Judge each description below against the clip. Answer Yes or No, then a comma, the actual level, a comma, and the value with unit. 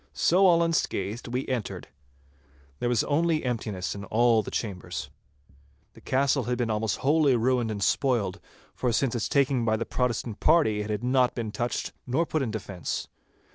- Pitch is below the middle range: Yes, low, 120 Hz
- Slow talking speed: No, average, 175 wpm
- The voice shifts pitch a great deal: No, average, 3.8 semitones